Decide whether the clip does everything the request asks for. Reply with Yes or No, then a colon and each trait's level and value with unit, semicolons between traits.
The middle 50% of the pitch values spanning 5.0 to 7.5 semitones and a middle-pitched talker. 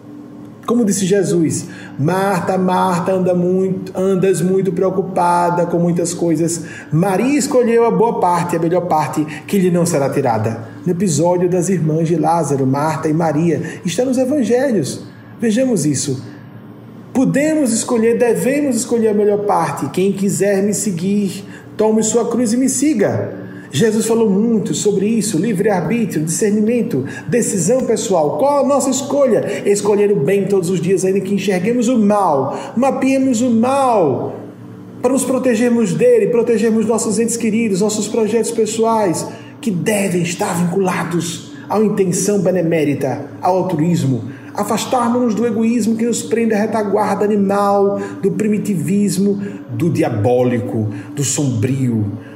No: average, 5.3 semitones; high, 195 Hz